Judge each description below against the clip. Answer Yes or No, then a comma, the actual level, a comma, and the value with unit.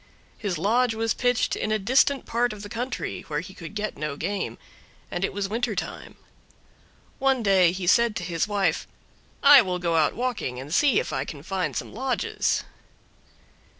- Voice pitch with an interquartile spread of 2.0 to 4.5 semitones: No, average, 5.3 semitones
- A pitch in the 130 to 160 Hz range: No, high, 205 Hz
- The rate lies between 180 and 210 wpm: Yes, average, 185 wpm